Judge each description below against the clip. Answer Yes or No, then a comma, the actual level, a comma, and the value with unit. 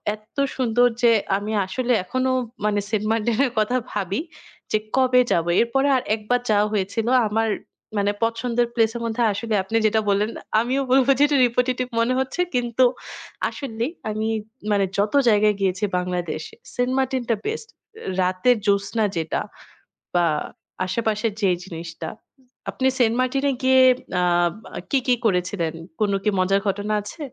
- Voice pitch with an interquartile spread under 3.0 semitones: No, average, 3.7 semitones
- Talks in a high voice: Yes, high, 225 Hz